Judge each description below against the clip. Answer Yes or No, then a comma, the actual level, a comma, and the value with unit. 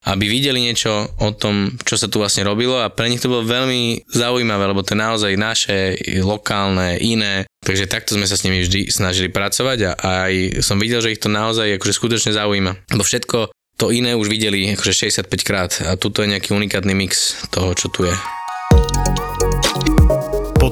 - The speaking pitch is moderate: No, low, 105 Hz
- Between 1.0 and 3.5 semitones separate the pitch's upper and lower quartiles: Yes, average, 2.7 semitones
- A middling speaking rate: No, fast, 180 wpm